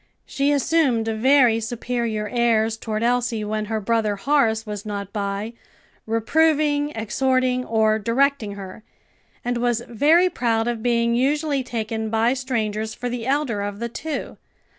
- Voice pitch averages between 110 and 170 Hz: No, high, 235 Hz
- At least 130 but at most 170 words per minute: Yes, average, 140 wpm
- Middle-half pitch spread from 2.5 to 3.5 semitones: Yes, average, 3.0 semitones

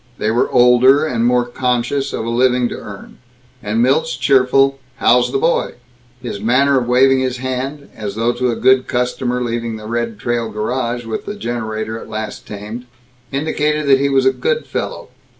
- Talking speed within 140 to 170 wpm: No, average, 185 wpm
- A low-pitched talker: Yes, low, 125 Hz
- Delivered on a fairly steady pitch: Yes, narrow, 2.3 semitones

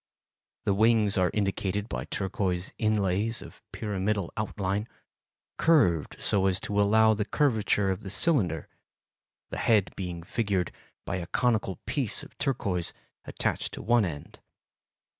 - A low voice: Yes, low, 100 Hz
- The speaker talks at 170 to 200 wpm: No, slow, 135 wpm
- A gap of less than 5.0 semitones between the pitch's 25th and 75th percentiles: Yes, average, 2.9 semitones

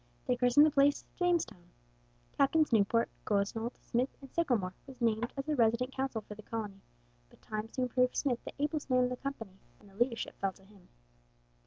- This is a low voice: No, high, 245 Hz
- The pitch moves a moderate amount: Yes, average, 4.2 semitones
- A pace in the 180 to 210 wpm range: Yes, average, 190 wpm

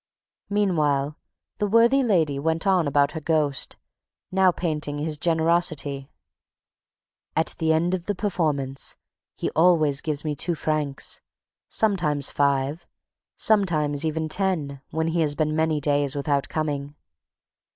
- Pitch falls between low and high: Yes, medium, 155 Hz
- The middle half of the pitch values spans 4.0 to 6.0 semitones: No, average, 3.2 semitones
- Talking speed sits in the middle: No, slow, 130 wpm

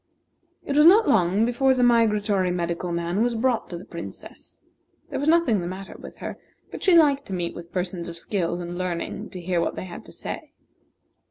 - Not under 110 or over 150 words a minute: No, fast, 205 wpm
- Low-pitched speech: No, high, 190 Hz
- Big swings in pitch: Yes, wide, 5.8 semitones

